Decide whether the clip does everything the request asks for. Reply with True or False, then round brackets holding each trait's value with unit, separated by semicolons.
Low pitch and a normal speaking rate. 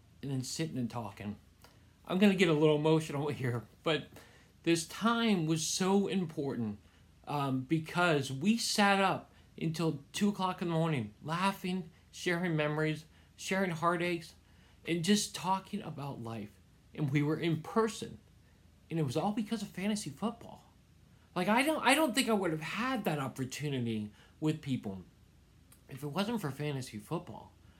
False (160 Hz; 155 wpm)